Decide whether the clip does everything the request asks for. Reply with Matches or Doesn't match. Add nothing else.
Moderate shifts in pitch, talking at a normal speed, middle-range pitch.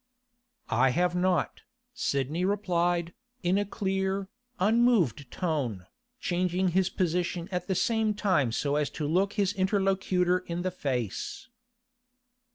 Doesn't match